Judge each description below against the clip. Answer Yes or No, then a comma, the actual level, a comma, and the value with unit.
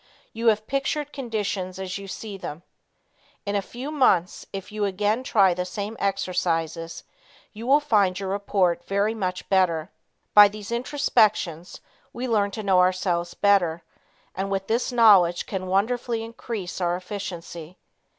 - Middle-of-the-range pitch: No, high, 200 Hz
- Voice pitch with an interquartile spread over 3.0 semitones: Yes, average, 3.4 semitones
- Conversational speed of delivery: Yes, average, 150 wpm